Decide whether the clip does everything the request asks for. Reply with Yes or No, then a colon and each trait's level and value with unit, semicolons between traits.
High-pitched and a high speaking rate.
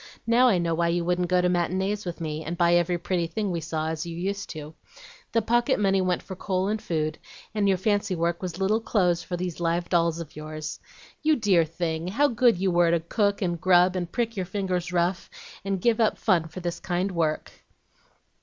No: medium, 180 Hz; fast, 220 wpm